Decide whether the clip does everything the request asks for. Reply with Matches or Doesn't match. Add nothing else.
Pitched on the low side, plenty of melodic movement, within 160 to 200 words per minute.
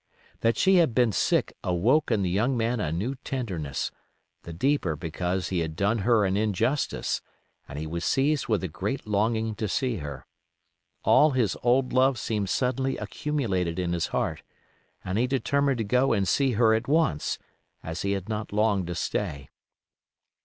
Matches